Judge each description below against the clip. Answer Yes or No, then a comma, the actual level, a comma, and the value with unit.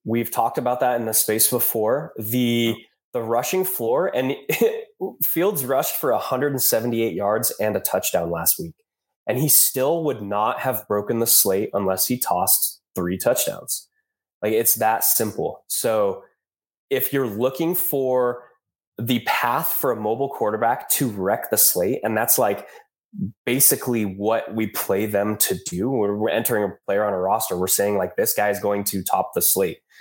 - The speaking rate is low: No, average, 170 wpm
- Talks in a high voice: No, low, 120 Hz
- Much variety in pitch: Yes, wide, 7.8 semitones